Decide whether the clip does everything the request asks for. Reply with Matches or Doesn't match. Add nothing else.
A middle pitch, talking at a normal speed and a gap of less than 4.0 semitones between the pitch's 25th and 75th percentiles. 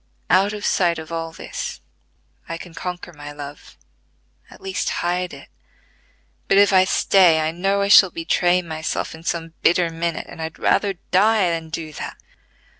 Matches